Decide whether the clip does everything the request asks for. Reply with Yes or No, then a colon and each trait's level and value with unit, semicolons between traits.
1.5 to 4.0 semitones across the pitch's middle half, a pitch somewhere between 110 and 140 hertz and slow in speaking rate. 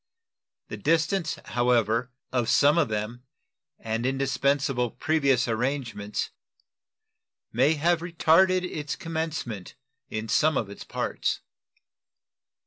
No: average, 5.3 semitones; low, 135 Hz; slow, 100 wpm